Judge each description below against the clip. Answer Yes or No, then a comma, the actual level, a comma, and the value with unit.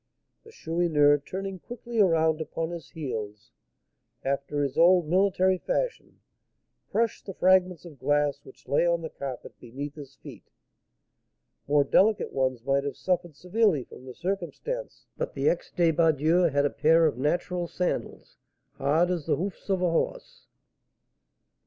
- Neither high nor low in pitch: Yes, medium, 165 Hz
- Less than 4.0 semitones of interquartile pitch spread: No, average, 4.4 semitones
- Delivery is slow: No, average, 145 wpm